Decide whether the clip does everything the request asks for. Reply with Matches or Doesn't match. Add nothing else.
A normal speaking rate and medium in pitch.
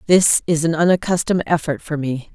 Matches